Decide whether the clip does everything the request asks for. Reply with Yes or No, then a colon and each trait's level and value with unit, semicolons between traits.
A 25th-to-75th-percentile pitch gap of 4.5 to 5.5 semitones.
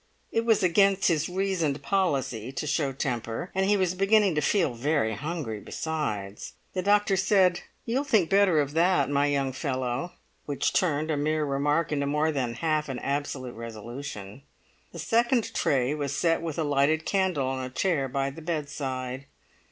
Yes: average, 5.2 semitones